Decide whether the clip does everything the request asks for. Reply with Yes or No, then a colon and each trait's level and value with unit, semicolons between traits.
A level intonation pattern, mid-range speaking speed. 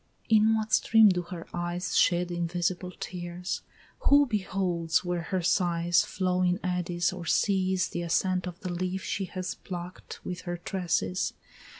Yes: narrow, 1.3 semitones; average, 155 wpm